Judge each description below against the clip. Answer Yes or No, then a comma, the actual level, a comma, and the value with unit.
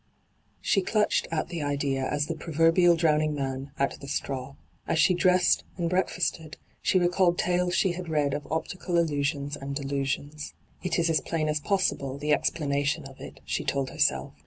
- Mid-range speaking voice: Yes, medium, 155 Hz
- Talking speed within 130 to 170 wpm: No, average, 180 wpm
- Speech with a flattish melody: No, average, 3.7 semitones